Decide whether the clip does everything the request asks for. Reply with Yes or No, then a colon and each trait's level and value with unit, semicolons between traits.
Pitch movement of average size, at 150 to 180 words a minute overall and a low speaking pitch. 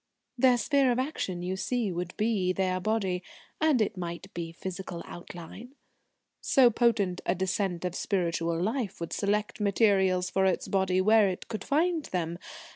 No: average, 3.9 semitones; average, 160 wpm; high, 190 Hz